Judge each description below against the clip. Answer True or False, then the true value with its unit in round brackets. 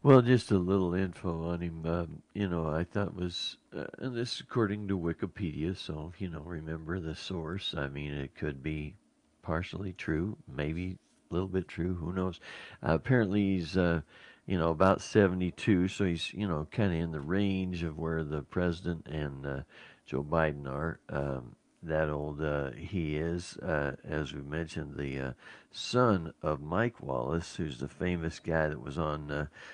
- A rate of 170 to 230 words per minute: True (185 wpm)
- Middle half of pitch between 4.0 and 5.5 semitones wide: False (3.6 semitones)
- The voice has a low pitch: True (85 Hz)